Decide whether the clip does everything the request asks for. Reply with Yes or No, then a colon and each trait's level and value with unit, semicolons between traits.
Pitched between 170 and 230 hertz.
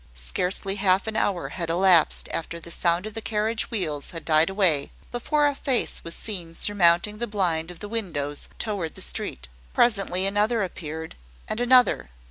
Yes: high, 190 Hz